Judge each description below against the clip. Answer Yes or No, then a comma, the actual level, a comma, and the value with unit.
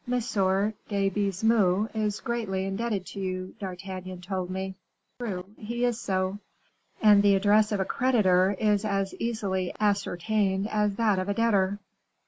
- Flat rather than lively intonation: Yes, narrow, 2.3 semitones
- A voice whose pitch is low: No, high, 200 Hz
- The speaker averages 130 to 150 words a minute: Yes, average, 140 wpm